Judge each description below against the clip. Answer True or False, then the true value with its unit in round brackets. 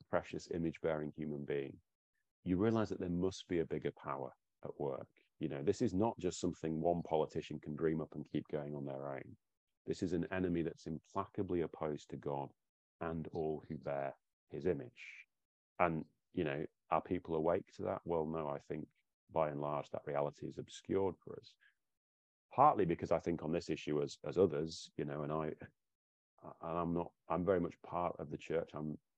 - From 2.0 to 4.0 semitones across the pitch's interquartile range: True (2.7 semitones)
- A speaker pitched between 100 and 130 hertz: False (80 Hz)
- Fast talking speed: False (195 wpm)